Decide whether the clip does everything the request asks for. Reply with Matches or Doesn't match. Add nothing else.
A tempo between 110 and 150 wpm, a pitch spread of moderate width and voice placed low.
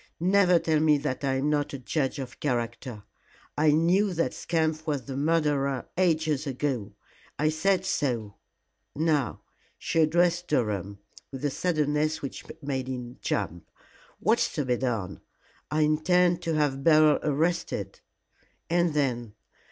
Doesn't match